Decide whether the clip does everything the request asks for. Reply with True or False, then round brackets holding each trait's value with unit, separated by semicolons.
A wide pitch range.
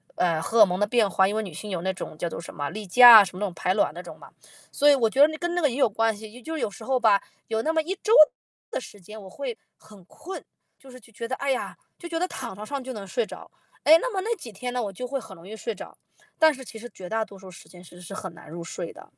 True (5.8 semitones)